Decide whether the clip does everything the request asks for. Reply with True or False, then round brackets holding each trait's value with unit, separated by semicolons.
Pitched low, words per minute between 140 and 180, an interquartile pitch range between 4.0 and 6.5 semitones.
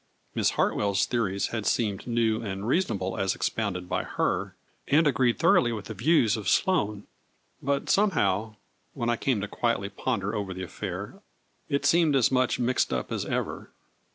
True (115 Hz; 170 wpm; 4.3 semitones)